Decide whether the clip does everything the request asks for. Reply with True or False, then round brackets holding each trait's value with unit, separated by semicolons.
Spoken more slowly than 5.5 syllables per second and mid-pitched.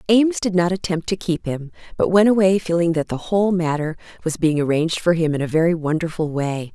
False (6.0 syllables/s; 170 Hz)